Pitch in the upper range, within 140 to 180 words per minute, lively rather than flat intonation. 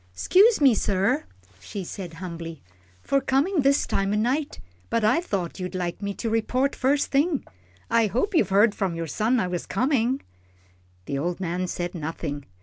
Yes: high, 205 Hz; average, 175 wpm; wide, 7.2 semitones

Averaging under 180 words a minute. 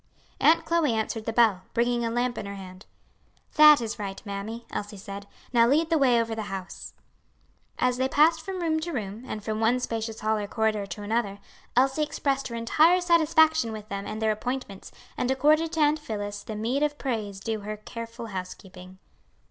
No: average, 195 wpm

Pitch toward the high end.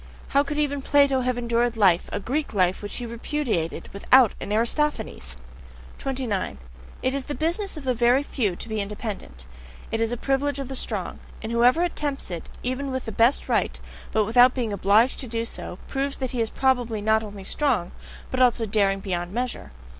Yes: high, 240 Hz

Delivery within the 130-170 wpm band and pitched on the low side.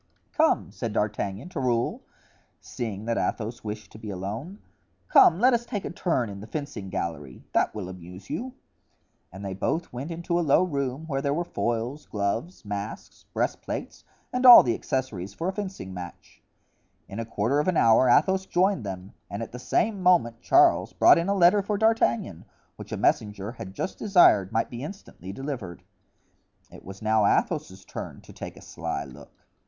No: average, 180 wpm; low, 120 Hz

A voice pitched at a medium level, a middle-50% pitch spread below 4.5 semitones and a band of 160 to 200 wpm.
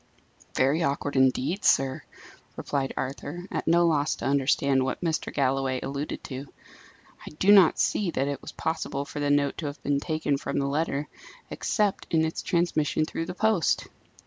Yes: medium, 145 Hz; average, 3.0 semitones; average, 175 wpm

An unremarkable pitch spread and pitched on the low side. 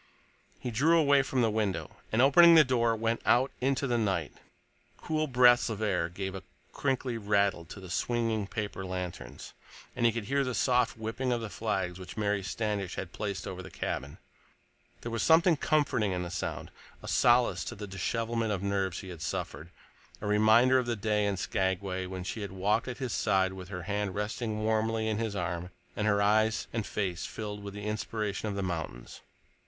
Yes: average, 3.7 semitones; low, 105 Hz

